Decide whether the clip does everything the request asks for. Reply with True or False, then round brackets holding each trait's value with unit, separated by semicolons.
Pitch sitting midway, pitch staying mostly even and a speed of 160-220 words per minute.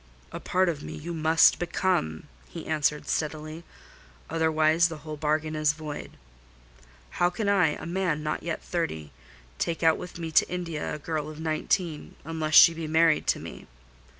True (160 Hz; 1.6 semitones; 170 wpm)